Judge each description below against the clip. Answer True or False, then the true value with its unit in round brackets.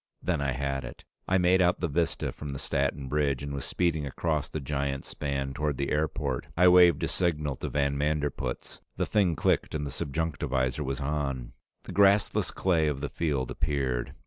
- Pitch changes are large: False (3.1 semitones)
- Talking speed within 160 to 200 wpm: True (190 wpm)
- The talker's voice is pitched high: False (75 Hz)